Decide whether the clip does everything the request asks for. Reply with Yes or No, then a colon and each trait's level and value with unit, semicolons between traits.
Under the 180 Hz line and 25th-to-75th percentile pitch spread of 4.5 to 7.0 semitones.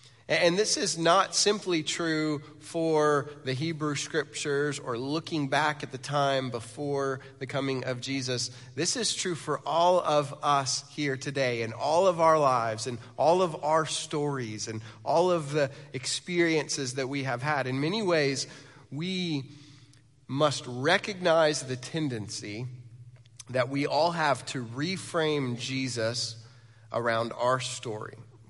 No: medium, 140 Hz; average, 3.6 semitones